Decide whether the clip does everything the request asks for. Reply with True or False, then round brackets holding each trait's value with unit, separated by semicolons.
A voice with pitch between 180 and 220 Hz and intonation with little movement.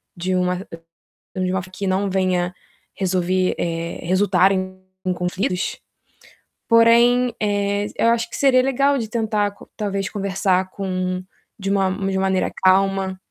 True (190 Hz; 1.9 semitones)